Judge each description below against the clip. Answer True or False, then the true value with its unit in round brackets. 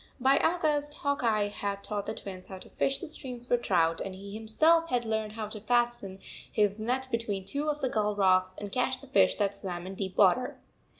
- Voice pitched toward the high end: True (220 Hz)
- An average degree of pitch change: True (4.5 semitones)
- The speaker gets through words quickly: True (220 wpm)